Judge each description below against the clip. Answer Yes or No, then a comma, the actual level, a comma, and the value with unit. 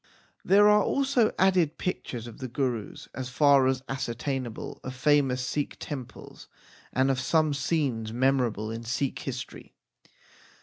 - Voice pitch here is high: No, low, 135 Hz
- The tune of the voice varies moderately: Yes, average, 3.2 semitones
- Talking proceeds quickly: No, slow, 135 wpm